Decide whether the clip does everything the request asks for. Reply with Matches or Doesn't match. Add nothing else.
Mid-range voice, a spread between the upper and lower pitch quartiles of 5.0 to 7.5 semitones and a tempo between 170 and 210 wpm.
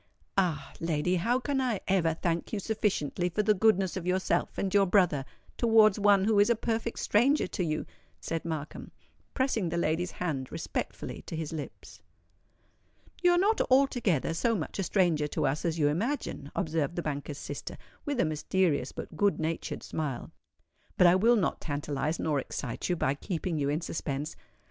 Matches